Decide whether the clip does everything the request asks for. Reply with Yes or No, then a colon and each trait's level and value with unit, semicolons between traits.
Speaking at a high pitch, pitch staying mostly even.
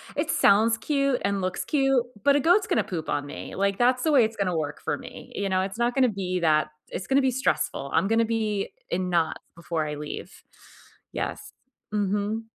No: high, 205 Hz; average, 5.2 semitones